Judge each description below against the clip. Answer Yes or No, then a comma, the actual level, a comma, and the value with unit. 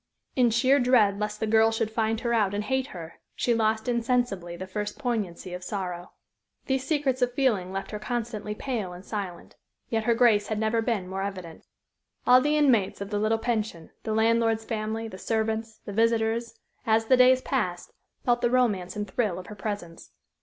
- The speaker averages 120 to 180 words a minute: No, average, 190 wpm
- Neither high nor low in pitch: No, high, 220 Hz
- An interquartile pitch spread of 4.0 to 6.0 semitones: No, average, 3.0 semitones